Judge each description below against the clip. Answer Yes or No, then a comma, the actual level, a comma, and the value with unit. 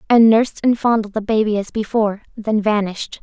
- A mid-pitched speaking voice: No, high, 215 Hz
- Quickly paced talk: No, average, 185 wpm